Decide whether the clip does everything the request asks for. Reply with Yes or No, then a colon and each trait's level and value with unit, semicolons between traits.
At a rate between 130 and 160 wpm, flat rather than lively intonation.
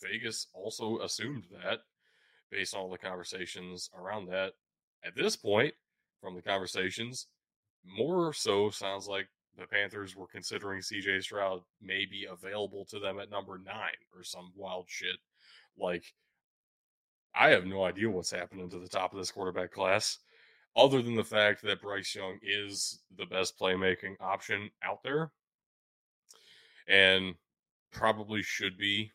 Yes: average, 145 wpm; narrow, 1.9 semitones